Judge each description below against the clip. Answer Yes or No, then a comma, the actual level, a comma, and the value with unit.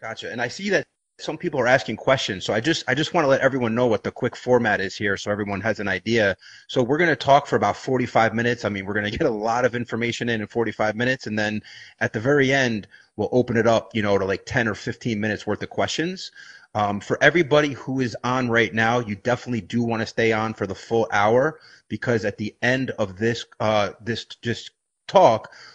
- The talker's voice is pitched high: No, low, 115 Hz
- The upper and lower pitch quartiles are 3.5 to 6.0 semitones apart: No, average, 2.7 semitones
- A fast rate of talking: Yes, fast, 240 wpm